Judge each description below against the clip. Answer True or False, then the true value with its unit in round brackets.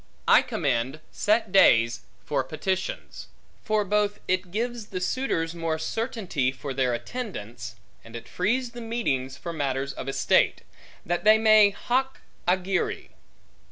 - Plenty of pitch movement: True (8.2 semitones)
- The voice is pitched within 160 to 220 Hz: True (185 Hz)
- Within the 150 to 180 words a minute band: False (135 wpm)